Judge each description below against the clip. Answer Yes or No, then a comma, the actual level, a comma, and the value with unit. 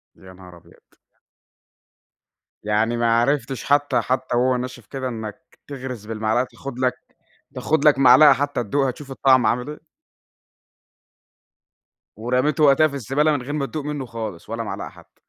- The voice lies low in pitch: Yes, low, 130 Hz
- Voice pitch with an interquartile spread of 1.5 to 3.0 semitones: No, average, 3.6 semitones